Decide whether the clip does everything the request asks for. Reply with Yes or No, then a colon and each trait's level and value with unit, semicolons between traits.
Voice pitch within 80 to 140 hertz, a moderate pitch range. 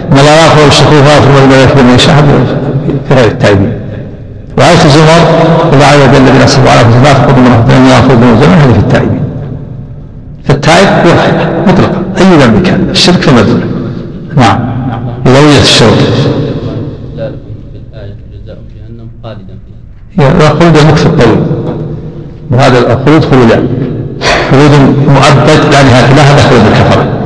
Yes: low, 135 Hz; average, 3.8 semitones